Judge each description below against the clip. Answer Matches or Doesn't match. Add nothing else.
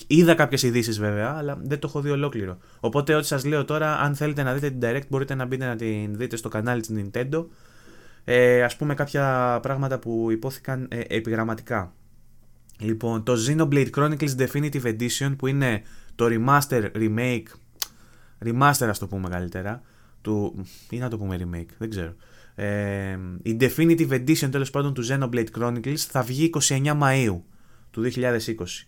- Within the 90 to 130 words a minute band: Doesn't match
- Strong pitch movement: Doesn't match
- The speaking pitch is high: Doesn't match